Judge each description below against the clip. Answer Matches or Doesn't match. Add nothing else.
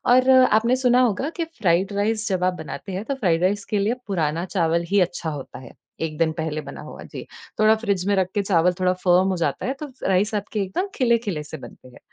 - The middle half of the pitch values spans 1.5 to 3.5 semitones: Doesn't match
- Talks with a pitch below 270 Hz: Matches